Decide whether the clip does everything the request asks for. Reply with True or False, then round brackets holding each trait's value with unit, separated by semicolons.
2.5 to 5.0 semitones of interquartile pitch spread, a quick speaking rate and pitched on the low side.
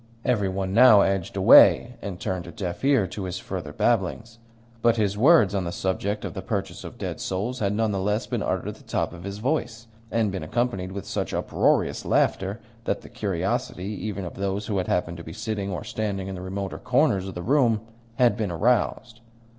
True (3.2 semitones; 210 wpm; 100 Hz)